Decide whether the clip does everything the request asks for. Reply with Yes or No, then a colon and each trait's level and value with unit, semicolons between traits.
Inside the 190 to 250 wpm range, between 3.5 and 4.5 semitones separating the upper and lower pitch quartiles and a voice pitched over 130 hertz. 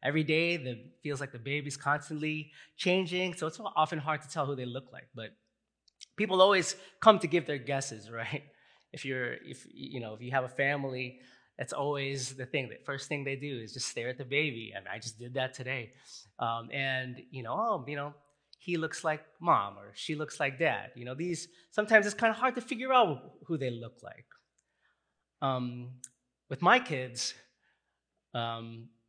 Yes: fast, 205 wpm; average, 3.9 semitones; medium, 140 Hz